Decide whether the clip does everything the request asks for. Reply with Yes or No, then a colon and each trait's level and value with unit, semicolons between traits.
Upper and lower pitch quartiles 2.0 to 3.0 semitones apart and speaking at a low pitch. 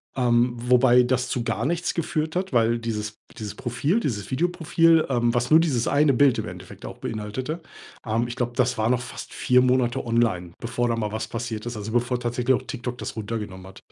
Yes: narrow, 2.4 semitones; low, 120 Hz